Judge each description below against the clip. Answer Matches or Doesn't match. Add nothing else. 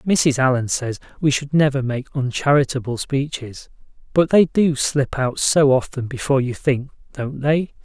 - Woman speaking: Doesn't match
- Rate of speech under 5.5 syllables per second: Matches